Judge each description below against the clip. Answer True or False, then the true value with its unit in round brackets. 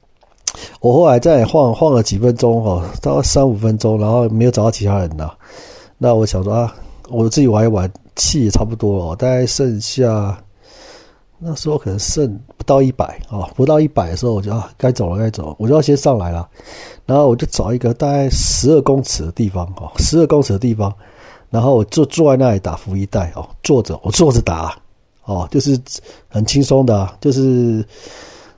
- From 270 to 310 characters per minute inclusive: True (275 characters per minute)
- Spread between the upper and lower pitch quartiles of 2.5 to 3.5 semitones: False (5.1 semitones)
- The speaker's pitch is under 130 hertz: True (115 Hz)